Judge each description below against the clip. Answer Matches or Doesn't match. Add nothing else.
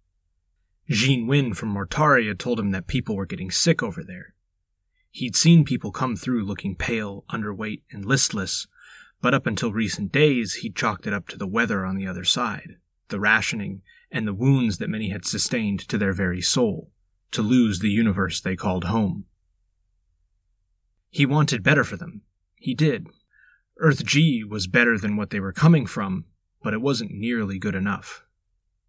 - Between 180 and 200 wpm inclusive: Doesn't match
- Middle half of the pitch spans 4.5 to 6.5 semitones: Matches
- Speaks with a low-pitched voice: Matches